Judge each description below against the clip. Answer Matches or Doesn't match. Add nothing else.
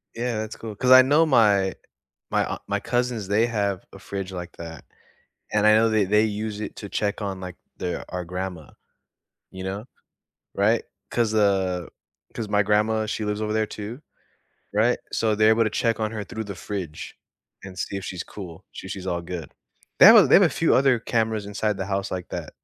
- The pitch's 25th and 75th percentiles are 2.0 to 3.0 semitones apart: Matches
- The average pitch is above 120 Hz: Doesn't match